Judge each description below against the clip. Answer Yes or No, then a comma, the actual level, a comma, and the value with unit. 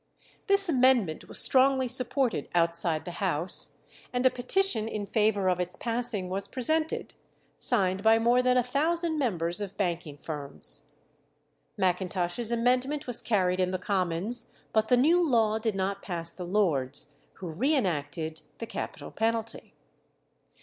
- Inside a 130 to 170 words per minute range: Yes, average, 145 wpm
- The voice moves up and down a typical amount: No, wide, 5.7 semitones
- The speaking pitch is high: Yes, high, 215 Hz